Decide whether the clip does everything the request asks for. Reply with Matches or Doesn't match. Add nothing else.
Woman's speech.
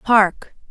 Matches